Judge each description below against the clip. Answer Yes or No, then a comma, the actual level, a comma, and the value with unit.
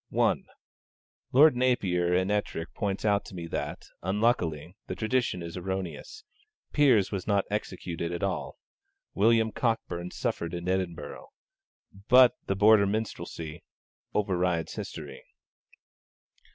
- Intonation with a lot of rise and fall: No, average, 4.2 semitones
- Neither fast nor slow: No, slow, 115 wpm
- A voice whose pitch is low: Yes, very low, 95 Hz